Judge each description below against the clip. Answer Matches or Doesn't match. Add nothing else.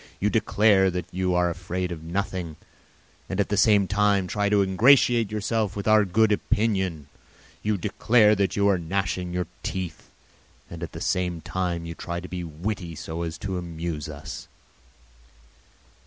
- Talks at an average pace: Matches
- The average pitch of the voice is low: Matches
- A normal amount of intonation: Matches